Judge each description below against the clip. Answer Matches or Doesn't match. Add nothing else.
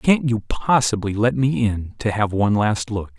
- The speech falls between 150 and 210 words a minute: Matches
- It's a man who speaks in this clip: Matches